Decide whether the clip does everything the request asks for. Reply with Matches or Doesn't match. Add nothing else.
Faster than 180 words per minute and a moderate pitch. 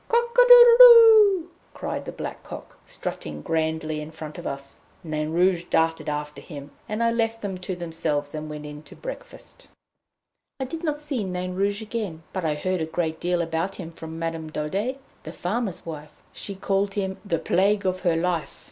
Matches